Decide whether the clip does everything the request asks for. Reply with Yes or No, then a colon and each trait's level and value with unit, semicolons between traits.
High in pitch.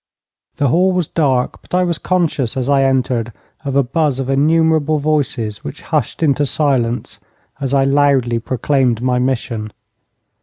No: low, 135 Hz